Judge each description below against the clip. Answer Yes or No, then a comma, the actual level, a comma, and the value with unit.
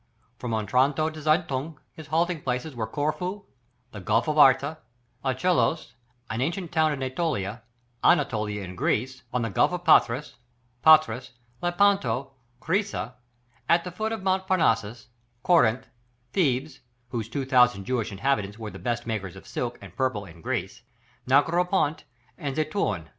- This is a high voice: No, low, 135 Hz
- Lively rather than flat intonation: Yes, wide, 5.9 semitones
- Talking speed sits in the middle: Yes, average, 145 wpm